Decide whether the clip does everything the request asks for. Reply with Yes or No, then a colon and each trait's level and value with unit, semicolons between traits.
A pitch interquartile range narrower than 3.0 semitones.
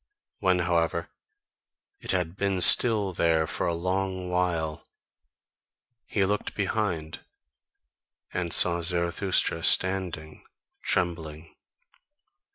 Yes: narrow, 2.4 semitones